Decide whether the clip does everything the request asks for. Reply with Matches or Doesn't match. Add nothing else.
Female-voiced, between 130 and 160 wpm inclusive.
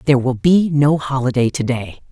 Doesn't match